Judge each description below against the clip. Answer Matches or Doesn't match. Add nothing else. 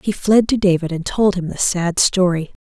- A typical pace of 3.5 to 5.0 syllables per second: Matches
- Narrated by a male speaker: Doesn't match